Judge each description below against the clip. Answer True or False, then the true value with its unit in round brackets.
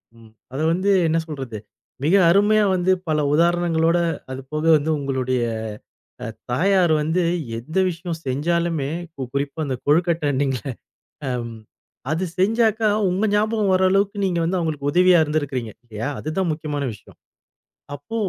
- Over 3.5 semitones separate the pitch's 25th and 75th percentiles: True (4.6 semitones)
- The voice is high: False (160 Hz)